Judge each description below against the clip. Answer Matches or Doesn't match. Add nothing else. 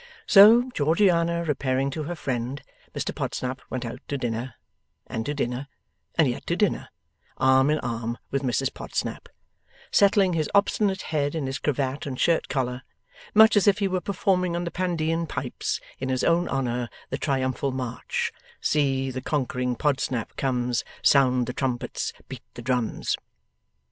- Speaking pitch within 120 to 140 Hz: Matches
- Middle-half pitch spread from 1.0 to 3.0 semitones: Doesn't match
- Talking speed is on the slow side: Doesn't match